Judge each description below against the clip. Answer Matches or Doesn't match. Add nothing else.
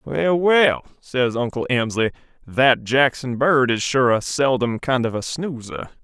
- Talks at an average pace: Matches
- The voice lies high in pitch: Doesn't match